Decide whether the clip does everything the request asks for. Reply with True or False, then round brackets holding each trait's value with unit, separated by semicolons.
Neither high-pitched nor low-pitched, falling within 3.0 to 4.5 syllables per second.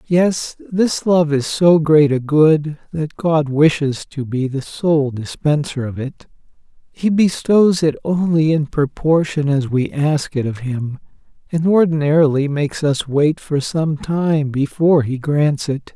True (150 Hz; 3.9 syllables/s)